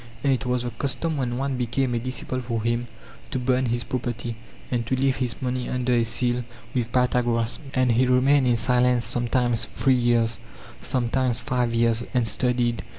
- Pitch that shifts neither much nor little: No, narrow, 1.3 semitones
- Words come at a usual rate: Yes, average, 180 wpm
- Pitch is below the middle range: Yes, low, 125 Hz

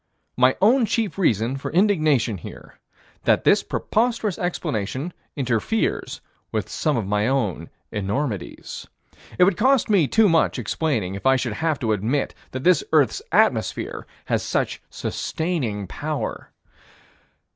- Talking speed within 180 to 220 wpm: No, slow, 135 wpm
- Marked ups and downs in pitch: Yes, wide, 8.5 semitones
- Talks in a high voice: No, medium, 140 Hz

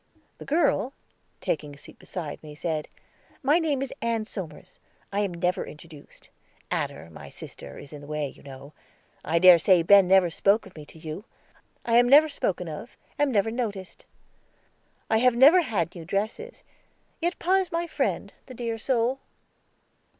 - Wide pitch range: Yes, wide, 7.7 semitones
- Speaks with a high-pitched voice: Yes, high, 200 Hz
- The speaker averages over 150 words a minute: Yes, average, 170 wpm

